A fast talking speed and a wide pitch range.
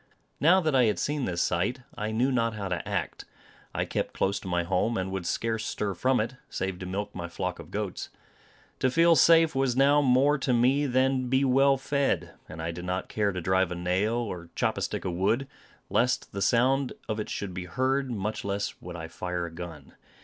Yes: fast, 220 wpm; wide, 6.4 semitones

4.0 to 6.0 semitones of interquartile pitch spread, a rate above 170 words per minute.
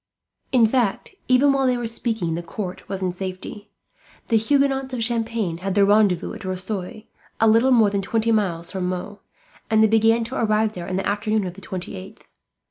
No: average, 3.5 semitones; average, 195 wpm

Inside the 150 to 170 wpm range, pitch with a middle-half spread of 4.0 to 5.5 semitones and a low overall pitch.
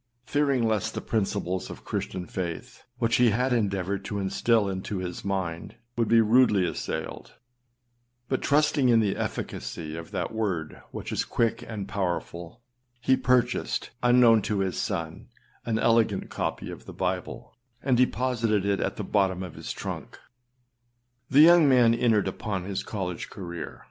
Yes: average, 155 wpm; average, 4.4 semitones; low, 105 Hz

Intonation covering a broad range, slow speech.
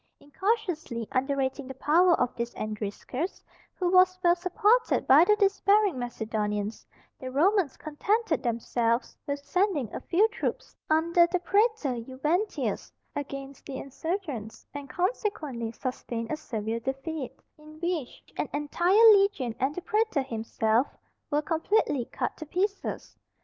Yes: wide, 6.5 semitones; slow, 130 wpm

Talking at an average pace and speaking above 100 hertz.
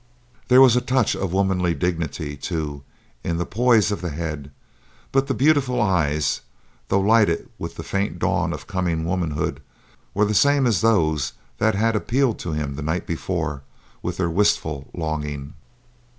No: average, 165 wpm; very low, 90 Hz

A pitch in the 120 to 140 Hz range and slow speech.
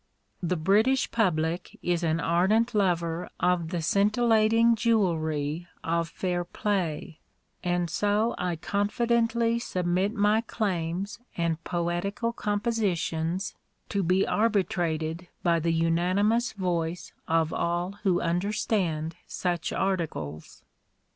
No: medium, 180 Hz; slow, 105 wpm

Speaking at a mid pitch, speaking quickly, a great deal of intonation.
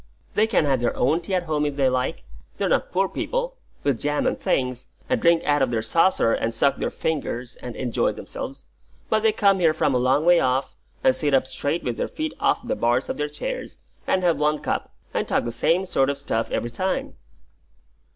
Yes: medium, 145 Hz; fast, 220 wpm; wide, 6.0 semitones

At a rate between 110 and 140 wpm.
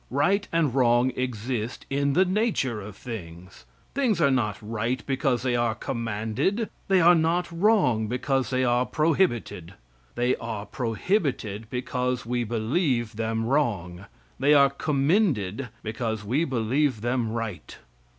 Yes: slow, 135 wpm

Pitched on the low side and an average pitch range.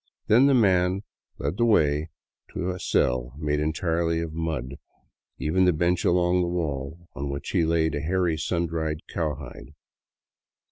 Yes: very low, 80 Hz; average, 3.2 semitones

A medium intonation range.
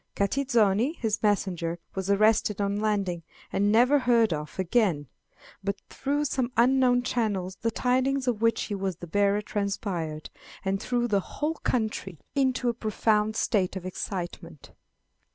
Yes: average, 4.1 semitones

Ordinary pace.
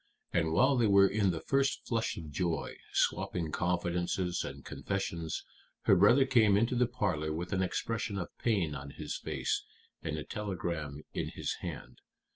Yes: average, 165 wpm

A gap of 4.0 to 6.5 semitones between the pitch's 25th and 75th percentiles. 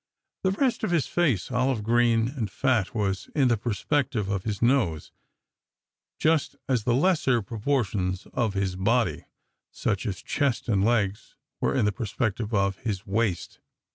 Yes: average, 4.6 semitones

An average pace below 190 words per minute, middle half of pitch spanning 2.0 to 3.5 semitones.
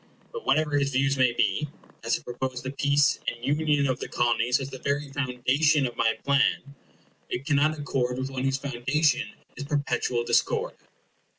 Yes: average, 175 wpm; narrow, 2.5 semitones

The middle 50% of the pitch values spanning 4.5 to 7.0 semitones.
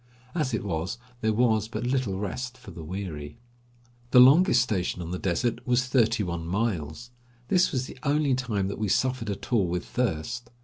Yes: wide, 5.4 semitones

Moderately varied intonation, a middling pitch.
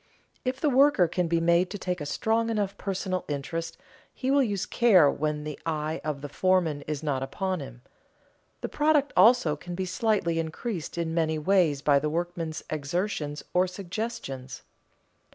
Yes: average, 4.6 semitones; medium, 170 Hz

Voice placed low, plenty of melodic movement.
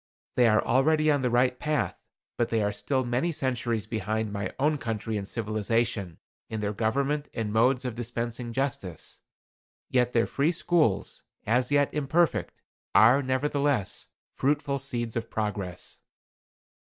No: low, 120 Hz; average, 4.1 semitones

